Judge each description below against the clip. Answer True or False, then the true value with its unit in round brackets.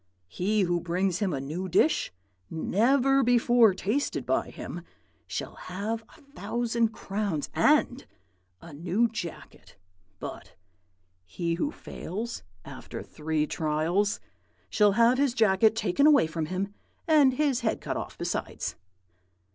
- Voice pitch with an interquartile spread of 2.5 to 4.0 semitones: False (5.3 semitones)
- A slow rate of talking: True (130 wpm)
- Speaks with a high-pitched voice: True (210 Hz)